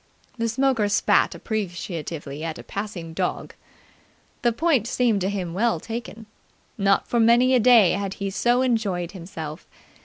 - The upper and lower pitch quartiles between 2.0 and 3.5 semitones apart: No, average, 4.9 semitones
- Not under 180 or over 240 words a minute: No, average, 150 wpm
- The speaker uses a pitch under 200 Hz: No, high, 205 Hz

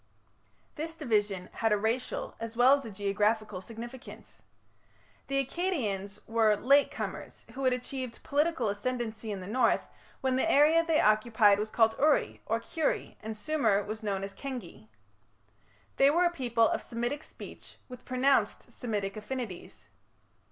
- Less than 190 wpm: Yes, average, 150 wpm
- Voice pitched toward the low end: No, high, 230 Hz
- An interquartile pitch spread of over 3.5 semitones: Yes, average, 4.3 semitones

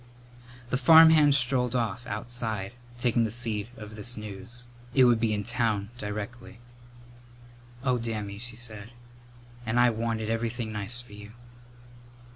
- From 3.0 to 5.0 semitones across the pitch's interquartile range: No, narrow, 2.4 semitones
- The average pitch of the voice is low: Yes, low, 115 Hz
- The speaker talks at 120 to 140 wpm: Yes, slow, 135 wpm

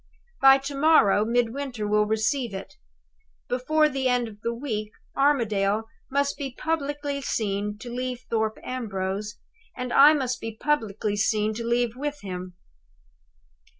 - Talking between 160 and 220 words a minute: No, average, 140 wpm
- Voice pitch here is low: No, high, 240 Hz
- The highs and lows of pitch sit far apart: No, average, 4.5 semitones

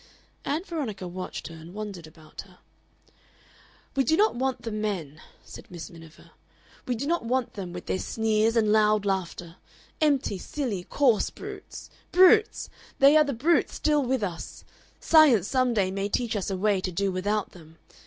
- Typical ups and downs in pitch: No, wide, 6.2 semitones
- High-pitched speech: Yes, high, 215 Hz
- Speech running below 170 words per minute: No, average, 175 wpm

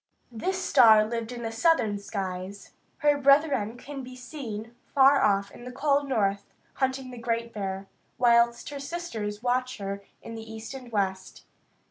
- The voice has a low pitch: No, high, 235 Hz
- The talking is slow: No, average, 160 wpm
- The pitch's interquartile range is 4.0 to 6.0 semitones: Yes, average, 4.3 semitones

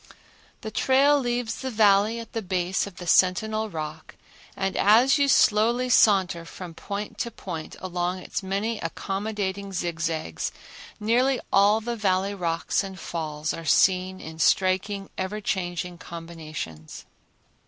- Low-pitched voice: No, high, 195 Hz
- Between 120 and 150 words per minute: Yes, slow, 135 wpm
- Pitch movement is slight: No, average, 3.8 semitones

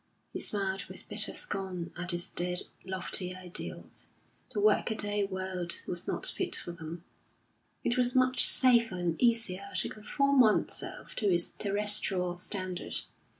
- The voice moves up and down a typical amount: Yes, average, 3.1 semitones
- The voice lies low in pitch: No, high, 190 Hz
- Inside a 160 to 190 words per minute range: No, average, 140 wpm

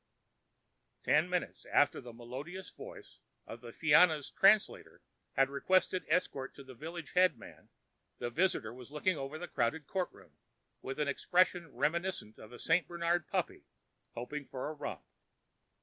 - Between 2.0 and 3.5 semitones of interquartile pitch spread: No, average, 5.2 semitones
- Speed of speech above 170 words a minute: No, average, 145 wpm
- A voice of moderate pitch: Yes, medium, 150 Hz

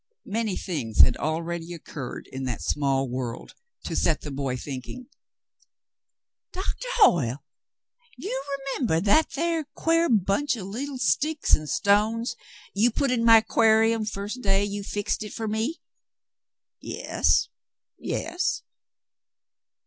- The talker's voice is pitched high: Yes, high, 205 Hz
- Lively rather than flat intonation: Yes, wide, 8.1 semitones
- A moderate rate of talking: No, slow, 130 wpm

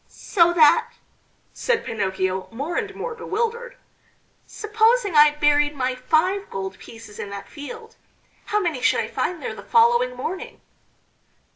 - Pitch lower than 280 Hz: No, very high, 335 Hz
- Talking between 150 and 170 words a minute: No, average, 140 wpm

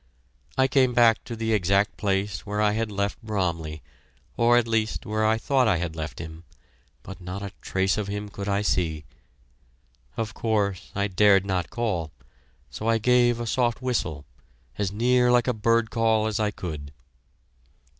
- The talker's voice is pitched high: No, low, 105 Hz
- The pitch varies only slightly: No, average, 3.2 semitones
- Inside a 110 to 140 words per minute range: No, average, 175 wpm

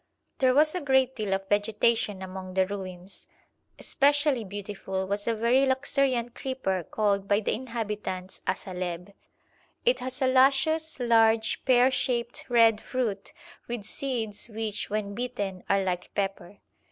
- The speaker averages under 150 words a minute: Yes, average, 140 wpm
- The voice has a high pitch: Yes, high, 220 Hz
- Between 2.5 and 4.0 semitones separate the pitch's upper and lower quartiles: No, average, 4.7 semitones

